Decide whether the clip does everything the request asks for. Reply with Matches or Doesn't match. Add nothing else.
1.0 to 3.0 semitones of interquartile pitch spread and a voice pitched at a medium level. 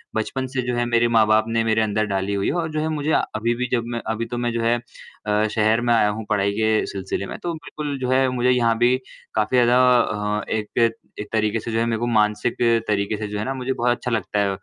Doesn't match